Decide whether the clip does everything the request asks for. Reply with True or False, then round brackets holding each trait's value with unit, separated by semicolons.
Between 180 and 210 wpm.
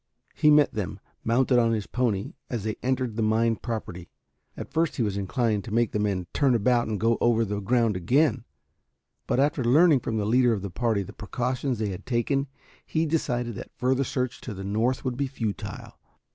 True (200 wpm)